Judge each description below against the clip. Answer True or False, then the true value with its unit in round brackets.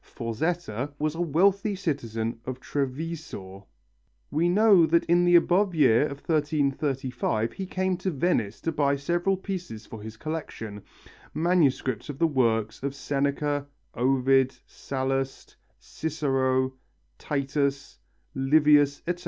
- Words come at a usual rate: False (120 wpm)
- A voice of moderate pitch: True (145 Hz)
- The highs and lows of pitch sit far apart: False (4.3 semitones)